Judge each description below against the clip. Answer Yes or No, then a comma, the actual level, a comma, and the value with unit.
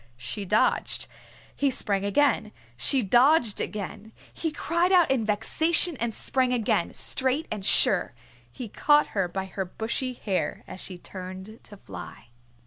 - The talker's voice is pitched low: No, high, 220 Hz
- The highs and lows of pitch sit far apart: Yes, wide, 5.7 semitones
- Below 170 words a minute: Yes, average, 145 wpm